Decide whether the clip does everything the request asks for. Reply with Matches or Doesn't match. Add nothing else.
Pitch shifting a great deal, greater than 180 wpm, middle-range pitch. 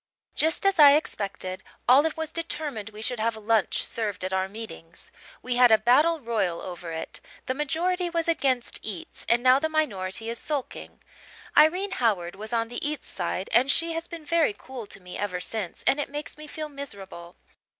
Doesn't match